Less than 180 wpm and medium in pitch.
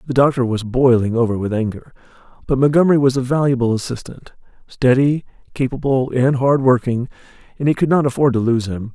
No: average, 155 wpm; low, 130 Hz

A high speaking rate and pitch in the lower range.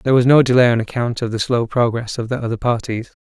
Yes: fast, 260 wpm; low, 120 Hz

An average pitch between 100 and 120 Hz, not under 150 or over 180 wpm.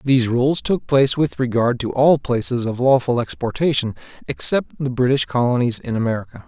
No: low, 130 Hz; average, 165 wpm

